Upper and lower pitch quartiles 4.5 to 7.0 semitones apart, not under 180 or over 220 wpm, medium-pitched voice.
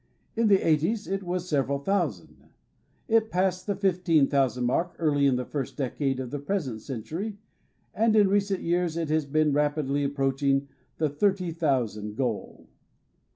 No: average, 5.2 semitones; average, 160 wpm; medium, 155 Hz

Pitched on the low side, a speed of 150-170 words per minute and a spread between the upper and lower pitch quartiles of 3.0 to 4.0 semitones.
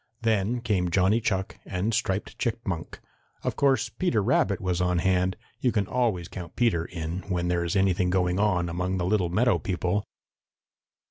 Yes: very low, 95 Hz; average, 165 wpm; average, 3.4 semitones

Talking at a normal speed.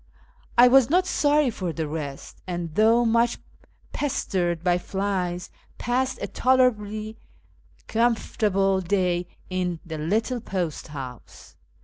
No: slow, 115 wpm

